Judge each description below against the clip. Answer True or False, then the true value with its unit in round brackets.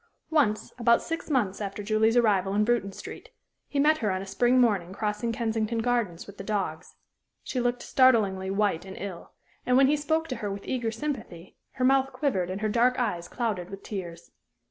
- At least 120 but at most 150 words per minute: False (195 wpm)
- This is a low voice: False (220 Hz)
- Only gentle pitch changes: False (4.3 semitones)